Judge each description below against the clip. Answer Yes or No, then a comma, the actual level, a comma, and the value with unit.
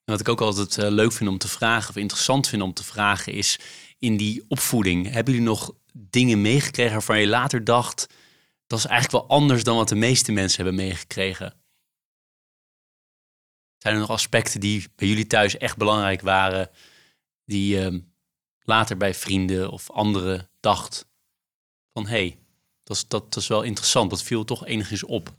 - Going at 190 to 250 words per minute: No, average, 175 wpm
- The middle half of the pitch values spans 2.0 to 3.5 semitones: Yes, average, 2.9 semitones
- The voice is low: Yes, low, 105 Hz